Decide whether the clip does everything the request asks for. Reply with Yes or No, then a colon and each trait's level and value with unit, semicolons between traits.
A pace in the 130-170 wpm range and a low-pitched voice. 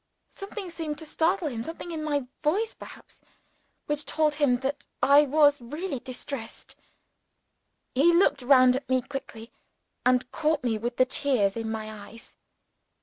No: average, 150 wpm; very high, 280 Hz